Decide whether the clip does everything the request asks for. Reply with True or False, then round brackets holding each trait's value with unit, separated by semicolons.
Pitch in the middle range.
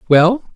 False (195 Hz)